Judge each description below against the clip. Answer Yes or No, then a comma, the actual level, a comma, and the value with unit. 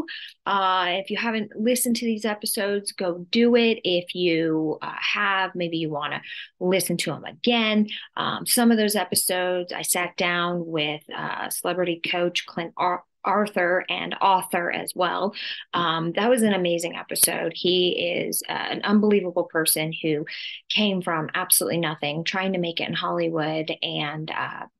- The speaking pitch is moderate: Yes, medium, 180 Hz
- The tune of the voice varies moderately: Yes, average, 3.7 semitones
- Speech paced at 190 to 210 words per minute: No, average, 160 wpm